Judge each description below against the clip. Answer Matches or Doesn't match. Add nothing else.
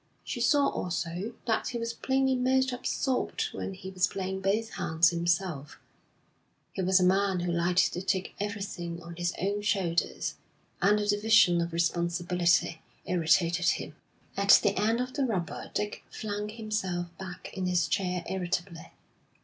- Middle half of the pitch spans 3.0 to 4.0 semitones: Matches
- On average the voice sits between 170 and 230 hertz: Matches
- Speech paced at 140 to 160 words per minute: Matches